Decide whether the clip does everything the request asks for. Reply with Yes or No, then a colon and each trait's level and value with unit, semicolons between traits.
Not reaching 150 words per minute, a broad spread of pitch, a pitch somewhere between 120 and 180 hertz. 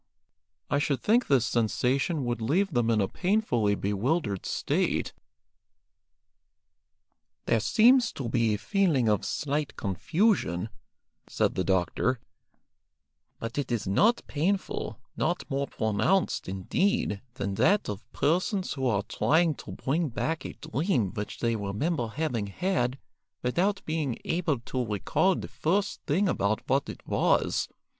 Yes: slow, 135 wpm; wide, 8.2 semitones; low, 135 Hz